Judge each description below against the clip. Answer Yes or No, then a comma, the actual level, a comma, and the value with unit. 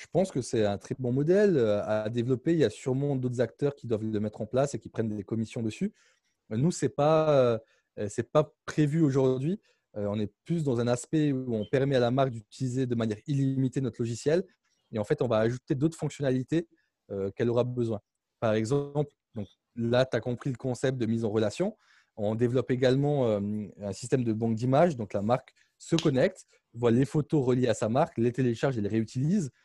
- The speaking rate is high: No, average, 210 wpm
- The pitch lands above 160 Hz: No, low, 125 Hz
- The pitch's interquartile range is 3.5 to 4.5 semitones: Yes, average, 4.2 semitones